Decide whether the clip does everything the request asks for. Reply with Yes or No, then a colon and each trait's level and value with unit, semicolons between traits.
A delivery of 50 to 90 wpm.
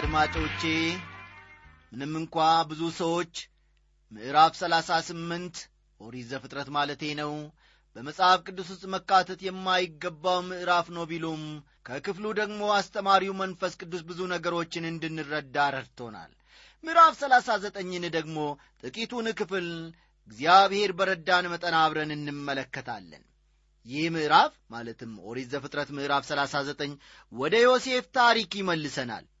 No: average, 105 wpm